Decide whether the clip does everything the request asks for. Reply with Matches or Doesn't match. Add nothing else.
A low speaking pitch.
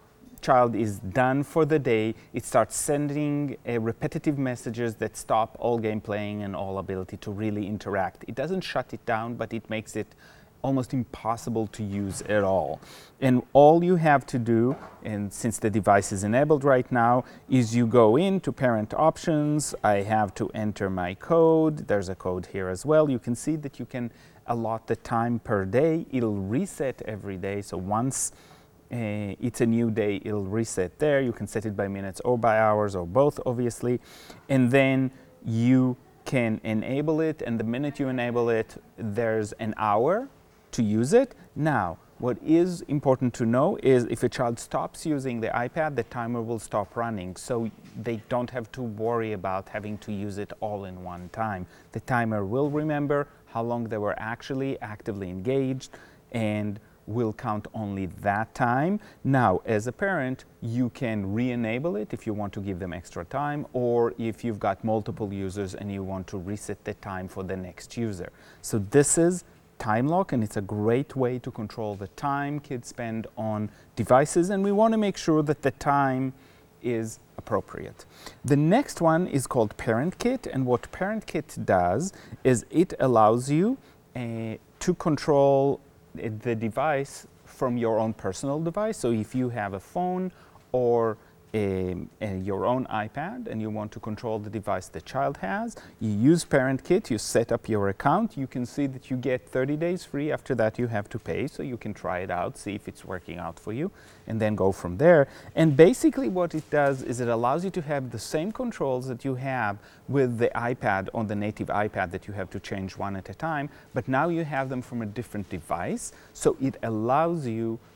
Matches